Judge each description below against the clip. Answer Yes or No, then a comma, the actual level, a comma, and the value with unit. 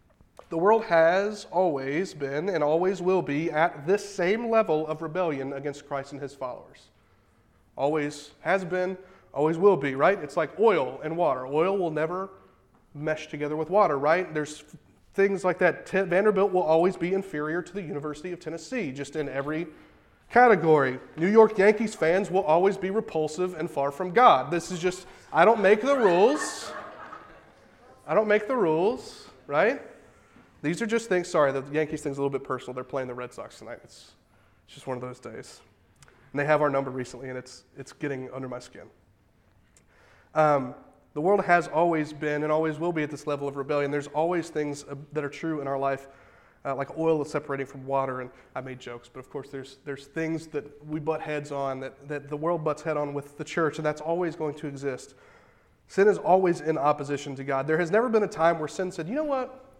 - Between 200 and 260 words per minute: Yes, fast, 205 wpm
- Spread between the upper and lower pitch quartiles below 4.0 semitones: No, average, 4.7 semitones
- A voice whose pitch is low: No, medium, 155 Hz